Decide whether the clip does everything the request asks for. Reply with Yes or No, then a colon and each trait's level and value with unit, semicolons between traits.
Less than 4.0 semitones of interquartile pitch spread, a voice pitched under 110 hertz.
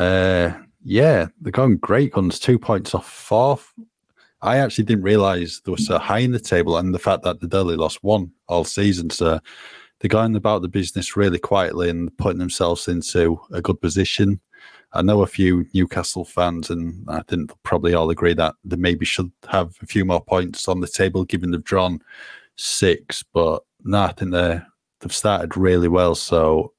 Yes: average, 2.9 semitones; very low, 90 Hz